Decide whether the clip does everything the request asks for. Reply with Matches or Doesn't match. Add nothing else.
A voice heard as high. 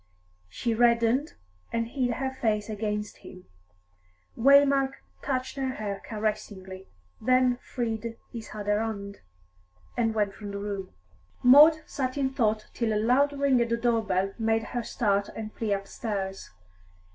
Matches